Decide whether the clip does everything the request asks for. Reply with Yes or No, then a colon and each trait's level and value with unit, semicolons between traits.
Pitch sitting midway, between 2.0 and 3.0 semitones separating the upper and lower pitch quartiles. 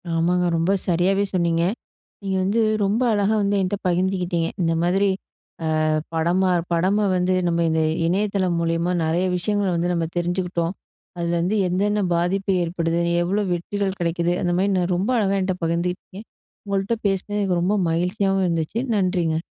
Yes: medium, 180 Hz; narrow, 2.4 semitones